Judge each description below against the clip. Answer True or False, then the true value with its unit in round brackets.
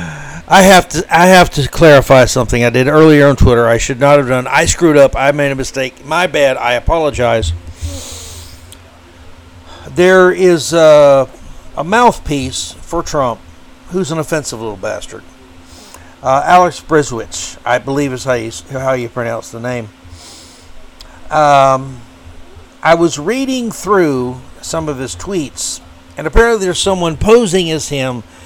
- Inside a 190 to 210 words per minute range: False (150 wpm)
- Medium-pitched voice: False (130 Hz)